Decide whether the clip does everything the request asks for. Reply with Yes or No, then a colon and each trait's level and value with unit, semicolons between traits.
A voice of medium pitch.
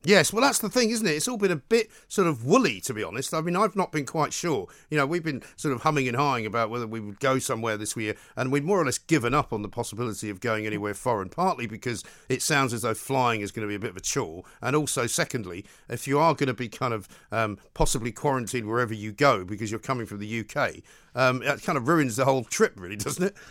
No: low, 130 Hz